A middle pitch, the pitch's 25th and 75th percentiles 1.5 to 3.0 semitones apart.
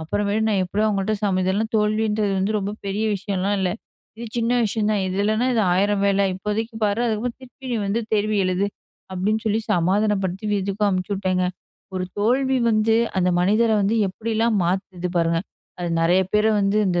No: high, 205 Hz; narrow, 2.5 semitones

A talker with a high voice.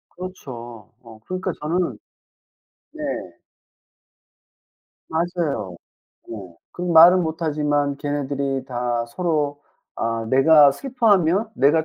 No: medium, 150 Hz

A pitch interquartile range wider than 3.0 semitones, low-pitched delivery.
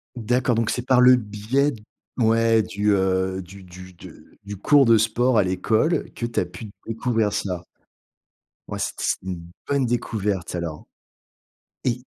Yes: average, 4.5 semitones; low, 110 Hz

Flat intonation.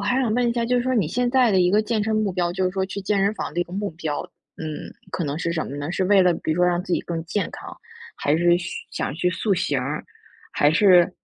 No: average, 3.9 semitones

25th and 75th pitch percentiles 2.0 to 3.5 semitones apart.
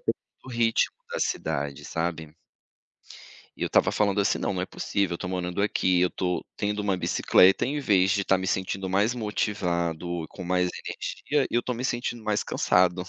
Yes: average, 2.9 semitones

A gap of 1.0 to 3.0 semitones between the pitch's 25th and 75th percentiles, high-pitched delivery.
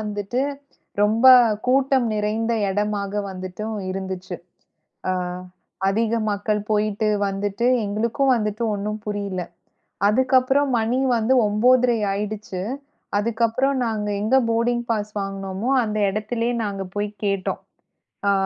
Yes: narrow, 2.4 semitones; high, 210 Hz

